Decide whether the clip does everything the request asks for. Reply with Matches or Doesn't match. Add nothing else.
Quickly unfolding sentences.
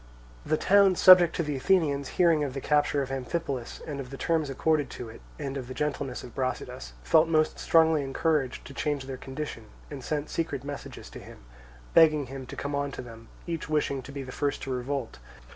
Matches